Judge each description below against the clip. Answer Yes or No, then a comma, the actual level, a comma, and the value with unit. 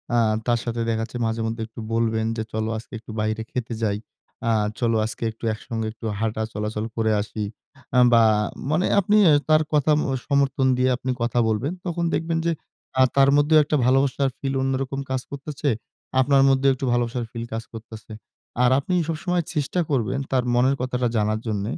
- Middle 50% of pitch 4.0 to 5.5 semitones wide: No, average, 3.6 semitones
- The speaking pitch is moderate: No, low, 125 Hz